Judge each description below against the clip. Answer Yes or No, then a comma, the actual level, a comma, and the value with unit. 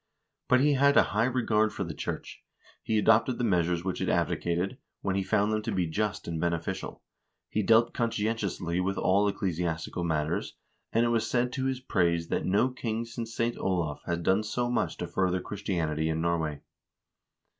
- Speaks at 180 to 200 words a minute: Yes, average, 185 wpm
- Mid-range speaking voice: No, low, 100 Hz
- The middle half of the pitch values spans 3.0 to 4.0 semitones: No, average, 5.1 semitones